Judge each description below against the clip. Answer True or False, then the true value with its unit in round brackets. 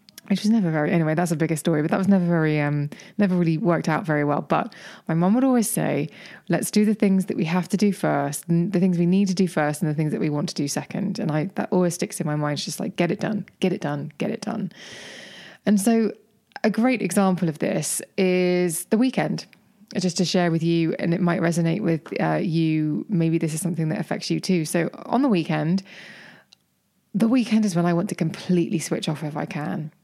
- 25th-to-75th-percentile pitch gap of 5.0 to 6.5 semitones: False (3.7 semitones)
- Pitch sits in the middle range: True (180 Hz)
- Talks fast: True (240 wpm)